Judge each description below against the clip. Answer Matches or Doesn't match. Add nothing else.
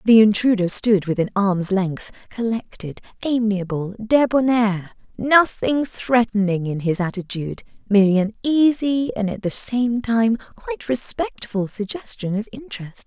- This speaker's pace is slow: Matches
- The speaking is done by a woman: Matches